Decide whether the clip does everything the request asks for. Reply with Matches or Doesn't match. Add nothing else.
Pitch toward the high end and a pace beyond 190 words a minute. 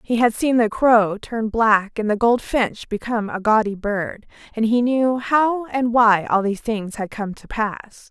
Matches